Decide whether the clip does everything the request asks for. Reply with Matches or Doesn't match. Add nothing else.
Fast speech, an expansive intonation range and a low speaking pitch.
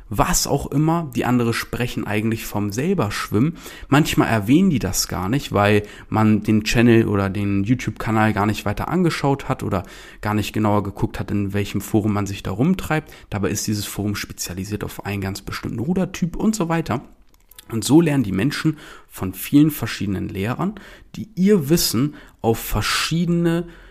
Doesn't match